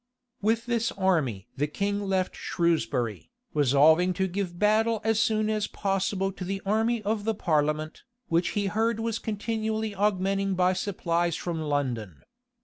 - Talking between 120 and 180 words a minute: Yes, average, 145 wpm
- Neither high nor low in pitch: No, high, 195 Hz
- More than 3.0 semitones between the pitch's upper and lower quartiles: Yes, average, 4.4 semitones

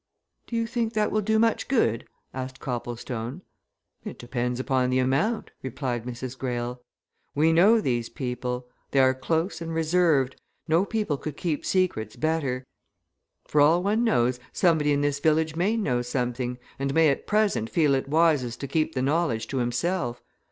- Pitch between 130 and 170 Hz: Yes, medium, 140 Hz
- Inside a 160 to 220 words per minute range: Yes, average, 165 wpm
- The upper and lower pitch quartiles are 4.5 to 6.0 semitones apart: Yes, average, 5.3 semitones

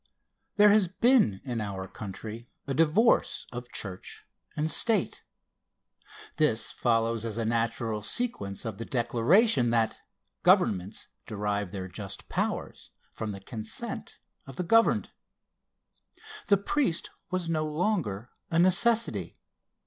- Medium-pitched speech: No, low, 120 Hz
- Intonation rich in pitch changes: Yes, wide, 8.9 semitones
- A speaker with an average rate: No, slow, 120 wpm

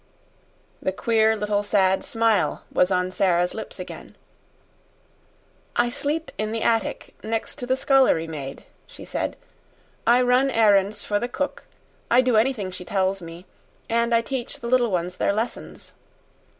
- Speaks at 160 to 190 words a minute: No, average, 150 wpm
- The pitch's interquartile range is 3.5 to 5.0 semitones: Yes, average, 4.2 semitones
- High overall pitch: Yes, high, 220 Hz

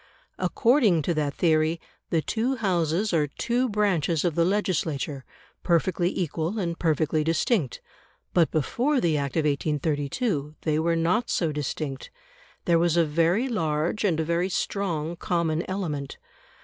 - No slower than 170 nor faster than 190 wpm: No, average, 145 wpm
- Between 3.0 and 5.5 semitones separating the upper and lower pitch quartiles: Yes, average, 3.6 semitones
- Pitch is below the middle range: No, medium, 165 Hz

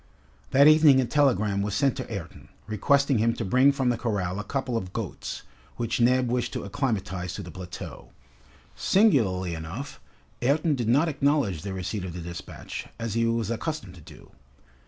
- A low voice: Yes, low, 115 Hz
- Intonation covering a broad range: Yes, wide, 6.3 semitones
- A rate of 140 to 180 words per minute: Yes, average, 175 wpm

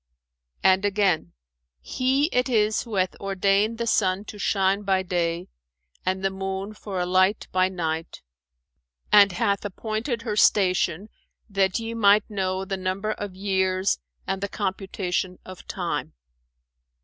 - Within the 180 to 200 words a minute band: No, average, 145 wpm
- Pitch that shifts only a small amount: Yes, narrow, 2.0 semitones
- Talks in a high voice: Yes, high, 195 Hz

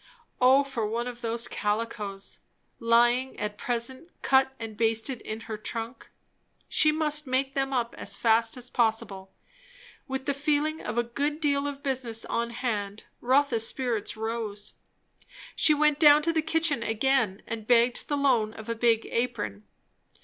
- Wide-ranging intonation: No, average, 3.6 semitones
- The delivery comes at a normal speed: Yes, average, 155 wpm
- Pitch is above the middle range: Yes, high, 240 Hz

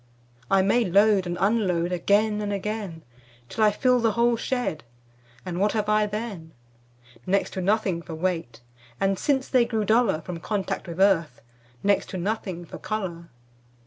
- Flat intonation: No, average, 3.6 semitones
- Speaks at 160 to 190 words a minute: Yes, average, 165 wpm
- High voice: Yes, high, 200 Hz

